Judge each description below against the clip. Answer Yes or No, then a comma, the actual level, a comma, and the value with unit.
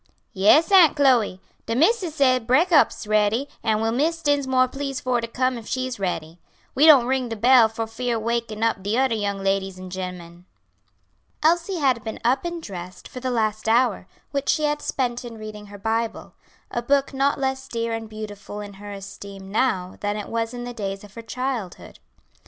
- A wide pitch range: No, average, 4.3 semitones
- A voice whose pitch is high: Yes, high, 230 Hz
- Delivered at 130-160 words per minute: No, average, 190 wpm